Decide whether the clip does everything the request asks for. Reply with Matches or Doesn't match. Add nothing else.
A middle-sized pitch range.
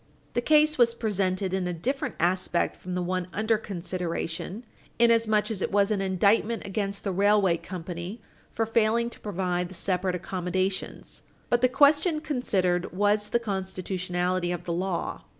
Matches